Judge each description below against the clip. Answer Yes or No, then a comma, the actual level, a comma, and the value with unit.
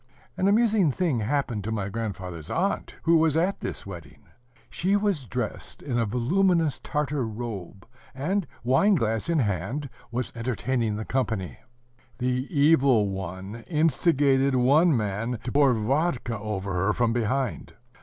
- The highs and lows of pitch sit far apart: Yes, wide, 5.9 semitones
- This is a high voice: No, low, 125 Hz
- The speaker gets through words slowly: No, average, 145 wpm